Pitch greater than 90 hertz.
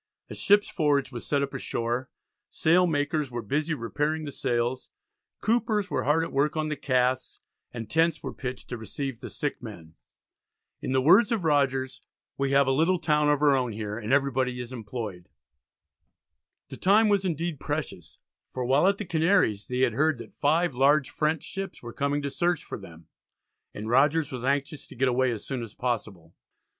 Yes: medium, 140 Hz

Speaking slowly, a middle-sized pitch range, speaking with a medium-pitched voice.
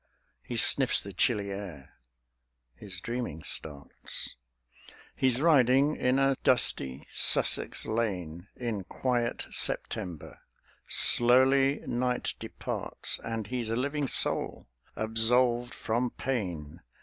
No: slow, 100 wpm; average, 5.0 semitones; low, 120 Hz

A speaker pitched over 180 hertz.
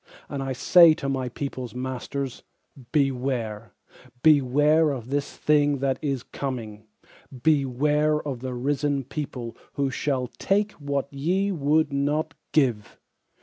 No: medium, 140 Hz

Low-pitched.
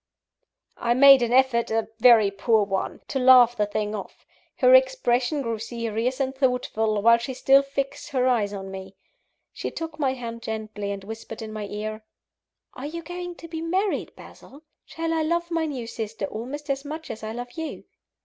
No: high, 245 Hz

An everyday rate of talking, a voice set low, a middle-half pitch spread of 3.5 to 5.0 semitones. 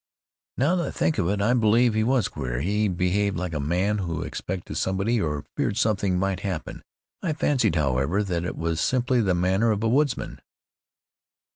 Yes: average, 185 wpm; low, 100 Hz; average, 4.5 semitones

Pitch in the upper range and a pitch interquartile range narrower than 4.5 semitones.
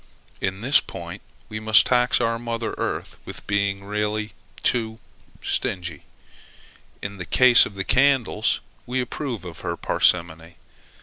No: low, 105 Hz; average, 3.9 semitones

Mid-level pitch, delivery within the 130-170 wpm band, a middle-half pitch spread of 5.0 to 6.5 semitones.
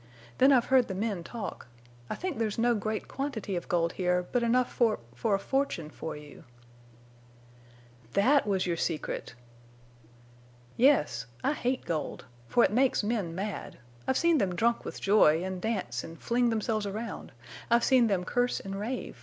No: high, 215 Hz; average, 155 wpm; average, 5.3 semitones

